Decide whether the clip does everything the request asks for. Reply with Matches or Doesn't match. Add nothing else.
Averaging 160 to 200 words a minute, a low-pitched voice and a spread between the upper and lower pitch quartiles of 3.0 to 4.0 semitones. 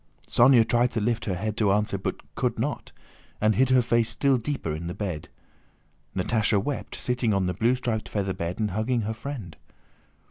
Matches